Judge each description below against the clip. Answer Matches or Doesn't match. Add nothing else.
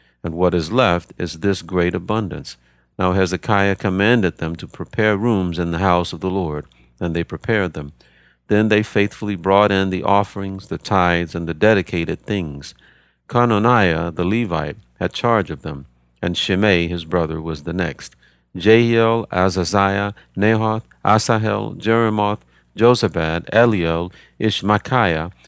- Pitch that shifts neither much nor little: Matches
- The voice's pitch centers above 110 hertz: Doesn't match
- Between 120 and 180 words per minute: Matches